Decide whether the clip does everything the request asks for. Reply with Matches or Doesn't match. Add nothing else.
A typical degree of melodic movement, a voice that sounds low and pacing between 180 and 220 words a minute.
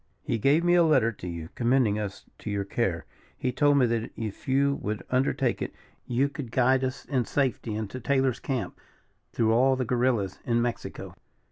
Matches